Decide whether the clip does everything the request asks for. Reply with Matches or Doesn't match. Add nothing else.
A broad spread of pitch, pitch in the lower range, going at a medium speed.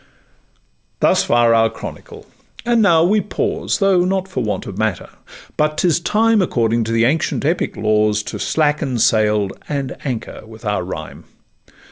Matches